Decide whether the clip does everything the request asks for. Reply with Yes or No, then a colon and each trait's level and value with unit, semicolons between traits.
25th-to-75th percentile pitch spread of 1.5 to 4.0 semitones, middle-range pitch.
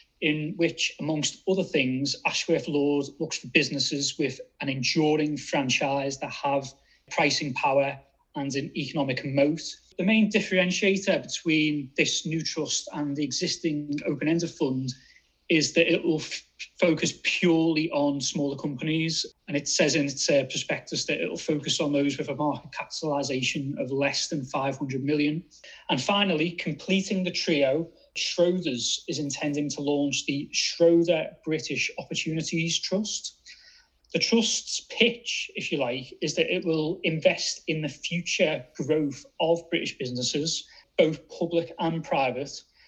Yes: average, 2.9 semitones; medium, 155 Hz